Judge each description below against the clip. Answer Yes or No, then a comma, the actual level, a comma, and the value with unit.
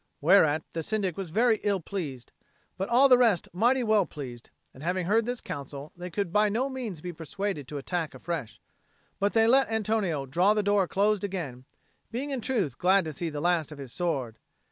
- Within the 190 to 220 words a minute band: Yes, average, 200 wpm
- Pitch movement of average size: No, wide, 5.8 semitones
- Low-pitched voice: No, medium, 185 Hz